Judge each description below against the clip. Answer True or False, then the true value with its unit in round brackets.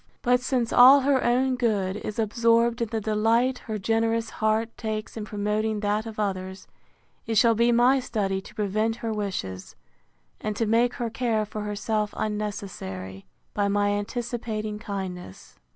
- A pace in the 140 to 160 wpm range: True (155 wpm)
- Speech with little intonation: True (2.2 semitones)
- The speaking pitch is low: False (215 Hz)